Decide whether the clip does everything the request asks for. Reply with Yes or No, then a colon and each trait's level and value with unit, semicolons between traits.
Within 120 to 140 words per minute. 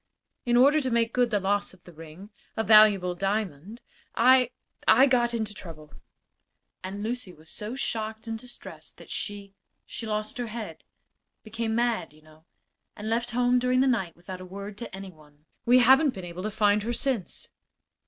No: average, 185 wpm